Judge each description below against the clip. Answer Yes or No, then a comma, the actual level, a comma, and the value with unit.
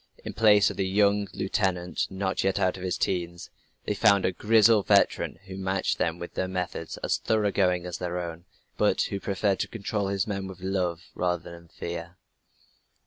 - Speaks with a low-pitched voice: Yes, very low, 95 Hz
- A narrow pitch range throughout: Yes, narrow, 2.2 semitones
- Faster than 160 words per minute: Yes, average, 185 wpm